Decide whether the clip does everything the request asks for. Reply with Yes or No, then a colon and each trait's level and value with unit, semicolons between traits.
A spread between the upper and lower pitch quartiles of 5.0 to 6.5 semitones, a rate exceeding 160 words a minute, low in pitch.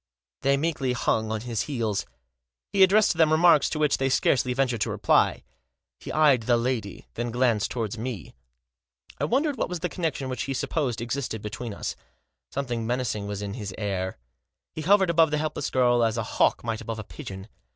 Yes: average, 5.3 semitones; average, 195 wpm; low, 125 Hz